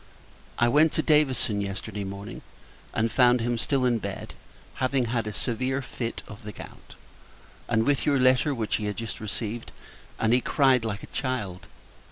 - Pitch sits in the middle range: No, low, 120 Hz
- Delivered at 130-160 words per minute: No, average, 175 wpm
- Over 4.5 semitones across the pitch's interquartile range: No, average, 3.2 semitones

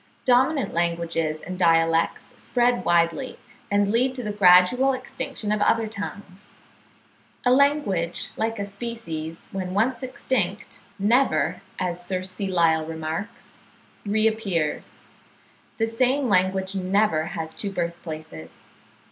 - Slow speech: Yes, slow, 120 wpm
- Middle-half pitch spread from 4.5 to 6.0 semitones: Yes, average, 5.3 semitones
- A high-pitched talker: Yes, high, 195 Hz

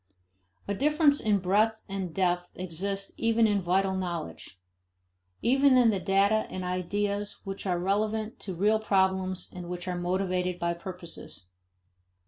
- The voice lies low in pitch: No, high, 195 Hz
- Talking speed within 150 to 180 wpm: No, average, 140 wpm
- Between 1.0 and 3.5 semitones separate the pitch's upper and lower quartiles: Yes, average, 2.8 semitones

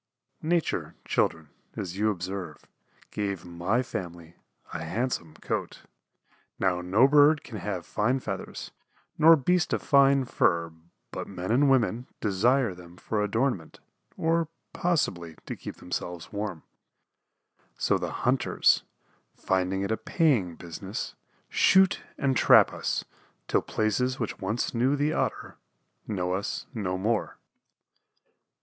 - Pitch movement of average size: No, wide, 6.4 semitones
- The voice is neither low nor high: No, low, 105 Hz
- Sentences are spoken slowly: Yes, slow, 125 wpm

